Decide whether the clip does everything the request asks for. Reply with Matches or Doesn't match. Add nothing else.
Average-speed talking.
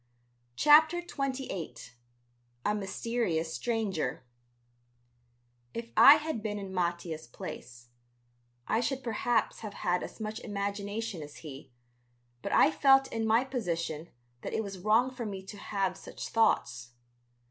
Doesn't match